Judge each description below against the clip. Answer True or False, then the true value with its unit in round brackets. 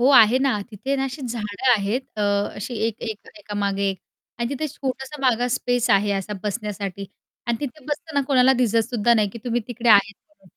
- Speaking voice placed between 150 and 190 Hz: False (235 Hz)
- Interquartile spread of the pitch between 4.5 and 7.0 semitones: False (3.9 semitones)